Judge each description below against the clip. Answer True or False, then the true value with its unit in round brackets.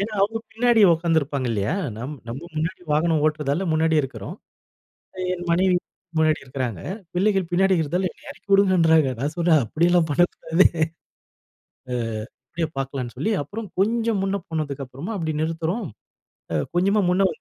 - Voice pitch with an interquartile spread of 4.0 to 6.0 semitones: True (4.4 semitones)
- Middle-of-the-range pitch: True (165 Hz)